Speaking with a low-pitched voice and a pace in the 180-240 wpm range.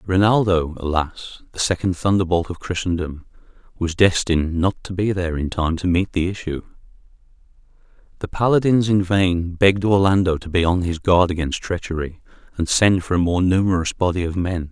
No: very low, 90 Hz; average, 165 wpm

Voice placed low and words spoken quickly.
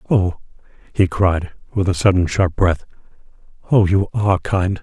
No: very low, 95 Hz; average, 150 wpm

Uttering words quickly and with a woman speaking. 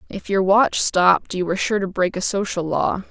Yes: fast, 230 wpm; female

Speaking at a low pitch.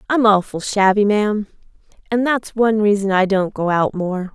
No: high, 205 Hz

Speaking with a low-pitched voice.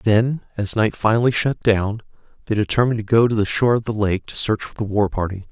Yes: low, 110 Hz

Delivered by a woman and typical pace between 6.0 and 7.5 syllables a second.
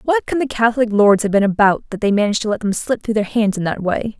Yes: female; 6.5 syllables/s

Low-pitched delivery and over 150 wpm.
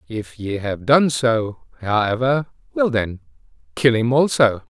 No: low, 120 Hz; average, 140 wpm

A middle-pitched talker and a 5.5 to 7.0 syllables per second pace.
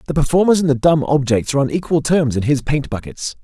Yes: medium, 145 Hz; 6.2 syllables/s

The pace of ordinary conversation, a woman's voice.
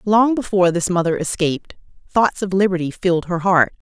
Yes: average, 170 wpm; female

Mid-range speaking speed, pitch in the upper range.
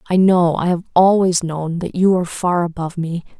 No: average, 175 wpm; medium, 175 Hz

